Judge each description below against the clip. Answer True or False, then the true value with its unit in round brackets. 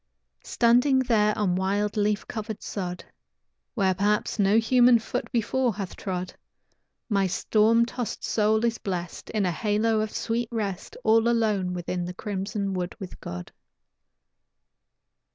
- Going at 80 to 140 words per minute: True (135 wpm)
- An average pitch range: True (3.0 semitones)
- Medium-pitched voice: False (210 Hz)